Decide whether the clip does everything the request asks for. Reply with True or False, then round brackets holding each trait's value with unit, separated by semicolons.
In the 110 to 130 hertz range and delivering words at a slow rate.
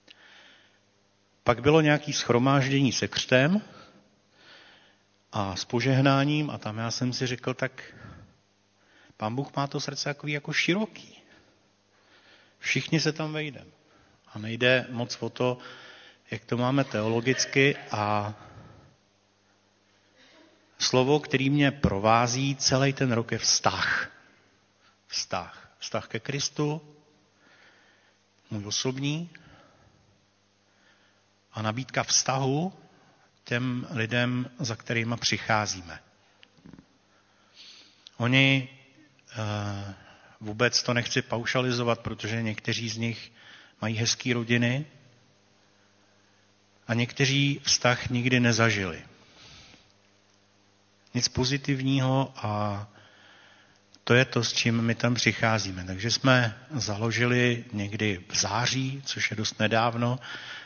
True (115 Hz; 100 wpm)